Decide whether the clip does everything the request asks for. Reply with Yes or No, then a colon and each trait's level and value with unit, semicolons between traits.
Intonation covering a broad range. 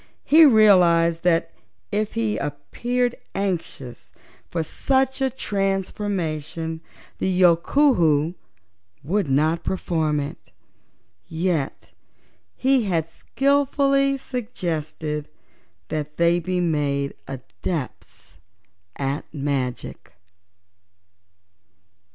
Yes: wide, 5.9 semitones